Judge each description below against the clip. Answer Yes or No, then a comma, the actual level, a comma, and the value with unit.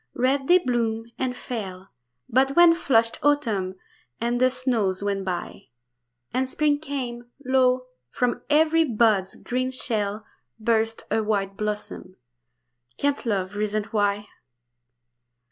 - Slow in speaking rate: Yes, slow, 120 wpm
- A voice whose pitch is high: Yes, high, 235 Hz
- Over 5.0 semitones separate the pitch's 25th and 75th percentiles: No, average, 3.9 semitones